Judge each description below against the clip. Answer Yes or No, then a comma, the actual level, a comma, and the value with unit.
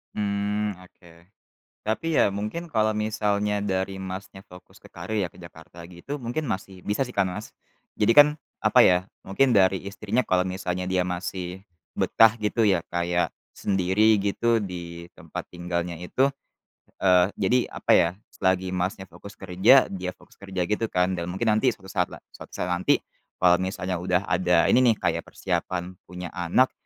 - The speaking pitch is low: Yes, very low, 95 Hz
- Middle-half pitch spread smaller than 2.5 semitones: No, average, 2.8 semitones